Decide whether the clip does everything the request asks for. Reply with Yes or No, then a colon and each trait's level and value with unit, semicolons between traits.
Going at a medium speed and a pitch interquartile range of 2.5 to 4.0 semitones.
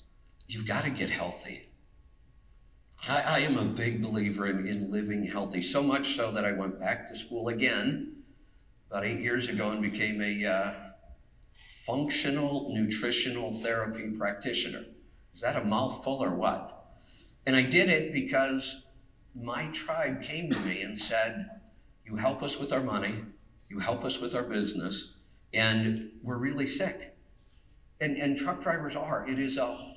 No: average, 160 wpm; average, 4.5 semitones